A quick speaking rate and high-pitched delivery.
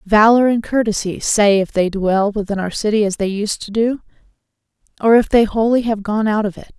Yes: fast, 210 wpm; high, 210 Hz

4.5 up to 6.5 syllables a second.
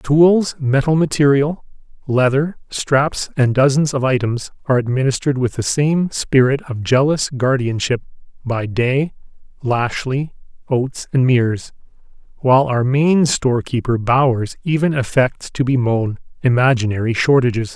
Yes: 4.6 syllables/s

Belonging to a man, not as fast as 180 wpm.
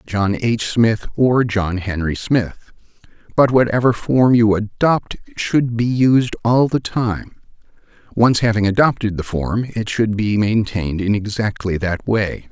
Yes: male; average, 150 wpm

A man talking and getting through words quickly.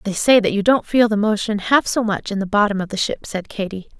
No: female; fast, 285 wpm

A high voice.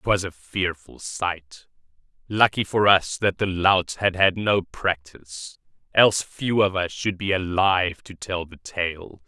No: very low, 90 Hz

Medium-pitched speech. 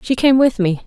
No: high, 235 Hz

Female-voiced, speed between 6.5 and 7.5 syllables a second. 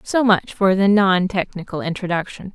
No: female; 4.9 syllables/s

